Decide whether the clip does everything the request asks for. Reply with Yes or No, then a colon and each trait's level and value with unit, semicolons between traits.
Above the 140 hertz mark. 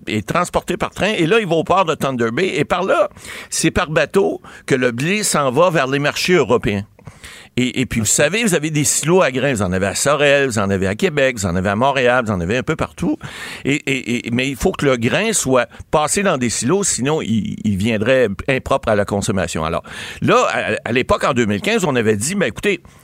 No: low, 135 Hz